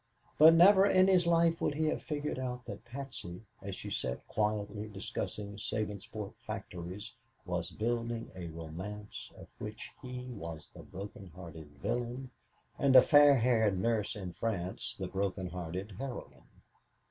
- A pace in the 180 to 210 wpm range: No, average, 145 wpm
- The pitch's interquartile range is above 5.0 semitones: Yes, wide, 5.4 semitones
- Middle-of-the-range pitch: No, low, 105 Hz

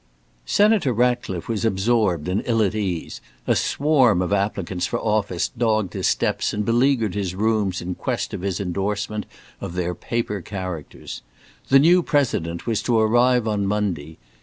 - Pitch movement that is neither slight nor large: Yes, average, 4.3 semitones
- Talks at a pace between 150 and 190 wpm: Yes, average, 160 wpm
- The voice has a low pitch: Yes, low, 105 Hz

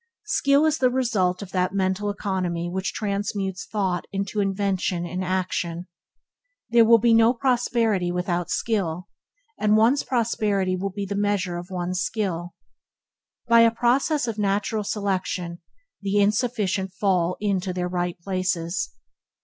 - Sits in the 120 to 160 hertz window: No, high, 195 Hz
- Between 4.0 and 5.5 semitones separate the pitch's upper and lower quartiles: No, average, 3.2 semitones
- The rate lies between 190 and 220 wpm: No, average, 145 wpm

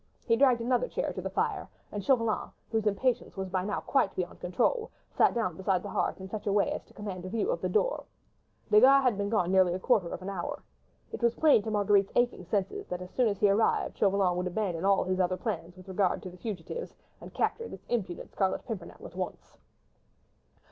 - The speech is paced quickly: Yes, fast, 225 wpm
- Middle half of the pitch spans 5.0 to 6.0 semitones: No, average, 3.7 semitones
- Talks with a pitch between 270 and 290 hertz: No, high, 200 Hz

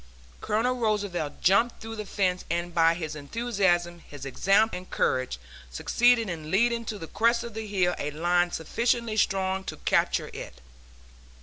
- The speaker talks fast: No, average, 160 wpm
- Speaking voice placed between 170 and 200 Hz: Yes, high, 190 Hz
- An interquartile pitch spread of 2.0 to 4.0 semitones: No, average, 4.6 semitones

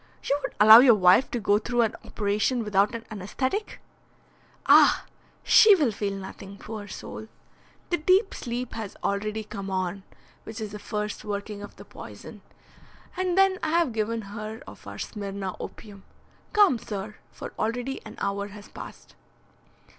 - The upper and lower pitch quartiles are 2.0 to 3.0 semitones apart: No, average, 3.4 semitones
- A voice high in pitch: Yes, high, 215 Hz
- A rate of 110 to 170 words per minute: Yes, average, 160 wpm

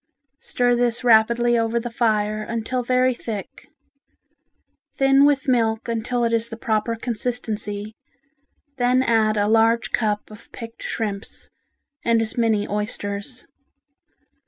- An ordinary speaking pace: No, slow, 125 wpm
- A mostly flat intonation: Yes, narrow, 2.1 semitones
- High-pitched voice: Yes, high, 230 Hz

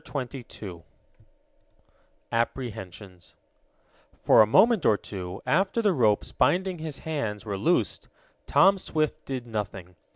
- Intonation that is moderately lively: No, wide, 7.7 semitones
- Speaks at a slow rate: Yes, slow, 120 wpm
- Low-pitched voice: Yes, low, 120 Hz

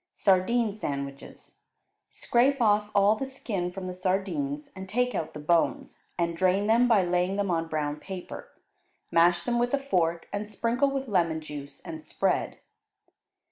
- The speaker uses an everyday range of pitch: No, wide, 5.8 semitones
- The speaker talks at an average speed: Yes, average, 160 wpm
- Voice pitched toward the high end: Yes, high, 195 Hz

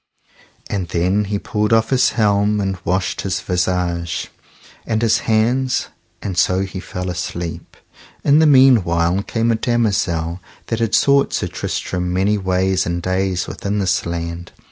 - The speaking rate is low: No, average, 150 wpm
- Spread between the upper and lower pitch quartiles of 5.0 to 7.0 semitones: No, average, 3.7 semitones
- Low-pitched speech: Yes, very low, 95 Hz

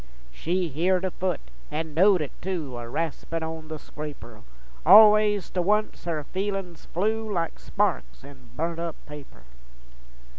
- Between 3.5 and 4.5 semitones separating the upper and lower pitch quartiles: Yes, average, 3.9 semitones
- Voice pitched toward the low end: No, medium, 170 Hz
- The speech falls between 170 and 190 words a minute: No, average, 150 wpm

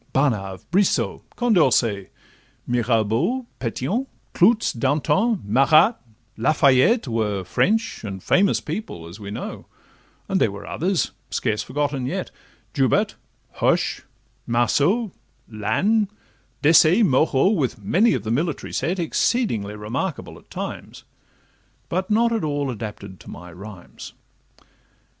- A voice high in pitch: No, low, 135 Hz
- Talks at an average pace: No, slow, 115 wpm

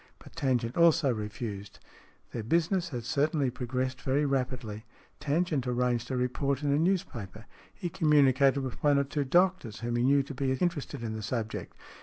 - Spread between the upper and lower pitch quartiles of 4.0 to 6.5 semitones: No, average, 3.6 semitones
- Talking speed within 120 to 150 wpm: No, average, 175 wpm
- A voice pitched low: Yes, low, 130 Hz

